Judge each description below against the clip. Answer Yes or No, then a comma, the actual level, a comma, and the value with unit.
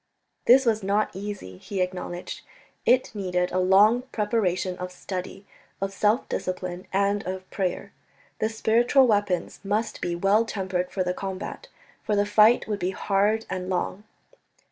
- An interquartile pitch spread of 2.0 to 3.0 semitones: Yes, average, 2.7 semitones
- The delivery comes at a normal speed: Yes, average, 150 wpm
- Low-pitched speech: No, high, 195 Hz